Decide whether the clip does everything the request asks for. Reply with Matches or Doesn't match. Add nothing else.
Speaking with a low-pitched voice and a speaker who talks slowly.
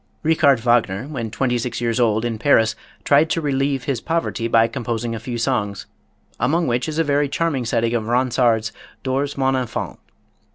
Doesn't match